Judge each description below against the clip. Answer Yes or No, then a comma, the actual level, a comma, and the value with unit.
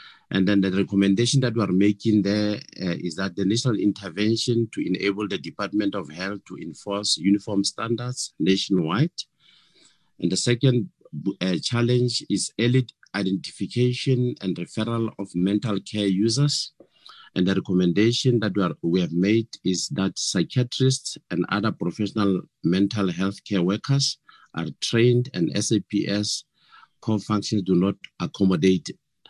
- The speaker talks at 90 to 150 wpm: Yes, average, 140 wpm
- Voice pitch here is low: Yes, low, 105 Hz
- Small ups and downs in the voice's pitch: No, average, 3.6 semitones